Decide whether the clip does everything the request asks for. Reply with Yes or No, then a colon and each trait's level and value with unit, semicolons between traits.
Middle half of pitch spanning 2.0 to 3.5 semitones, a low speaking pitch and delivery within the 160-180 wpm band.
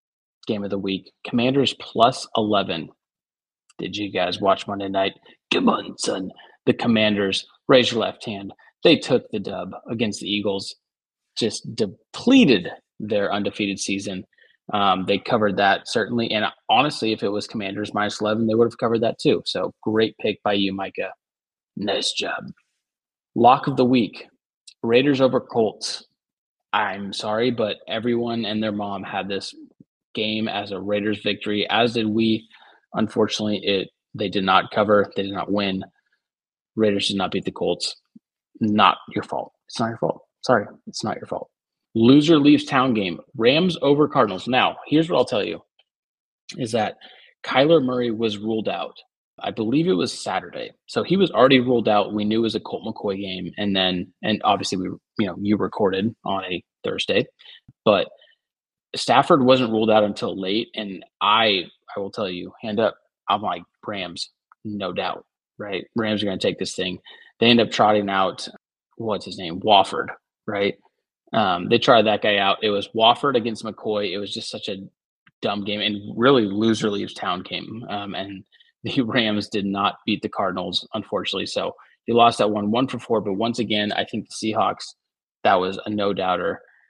Yes: narrow, 2.5 semitones; low, 105 Hz; average, 175 wpm